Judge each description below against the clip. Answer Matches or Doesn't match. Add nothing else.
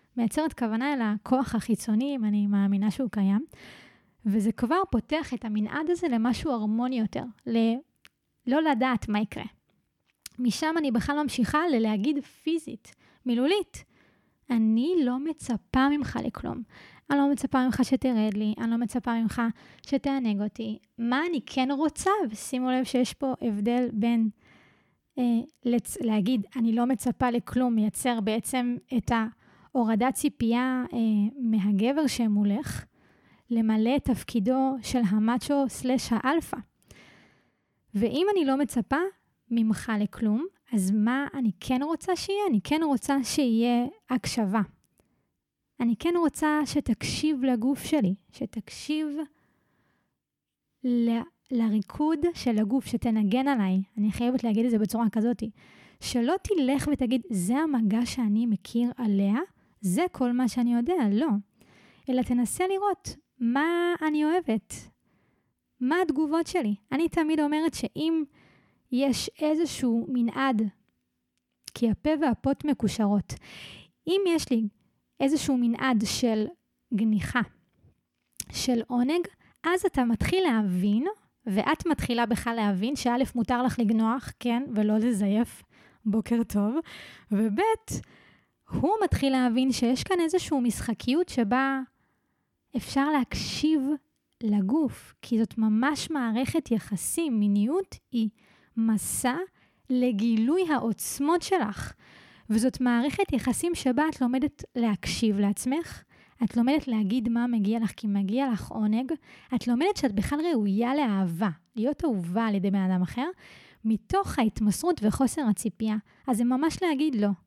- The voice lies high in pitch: Matches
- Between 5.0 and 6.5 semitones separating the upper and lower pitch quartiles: Doesn't match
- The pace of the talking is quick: Doesn't match